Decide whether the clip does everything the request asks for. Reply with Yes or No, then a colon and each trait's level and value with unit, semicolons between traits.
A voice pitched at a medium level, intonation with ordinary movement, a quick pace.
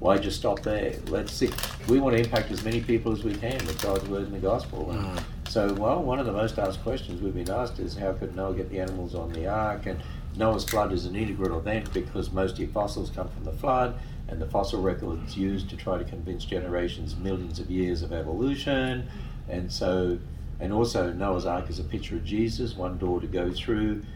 No: very low, 95 Hz; average, 3.6 semitones; fast, 225 wpm